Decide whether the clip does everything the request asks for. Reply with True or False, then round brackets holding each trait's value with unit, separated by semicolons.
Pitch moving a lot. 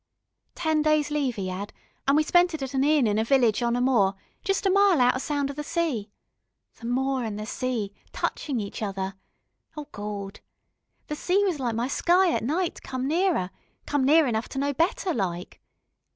True (5.8 semitones)